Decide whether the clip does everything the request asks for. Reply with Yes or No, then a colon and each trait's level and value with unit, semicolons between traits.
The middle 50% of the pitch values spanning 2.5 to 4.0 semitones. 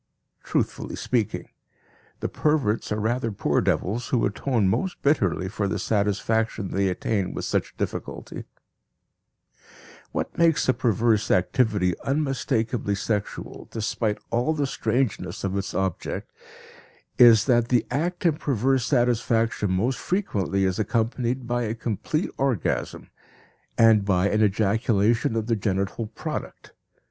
Yes: average, 3.7 semitones